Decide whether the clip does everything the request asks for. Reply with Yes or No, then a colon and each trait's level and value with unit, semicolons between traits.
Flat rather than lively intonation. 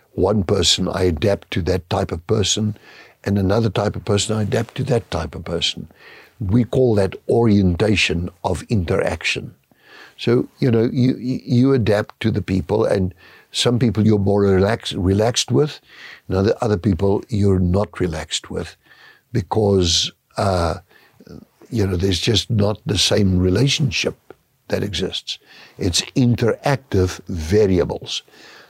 No: average, 3.5 semitones